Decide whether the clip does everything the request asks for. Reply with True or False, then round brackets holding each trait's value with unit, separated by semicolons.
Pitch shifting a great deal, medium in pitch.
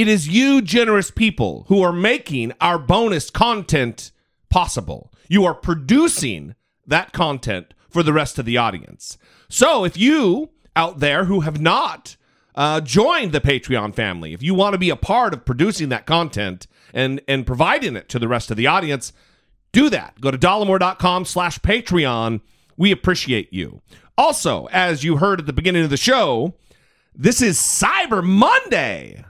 True (7.0 semitones; 165 Hz)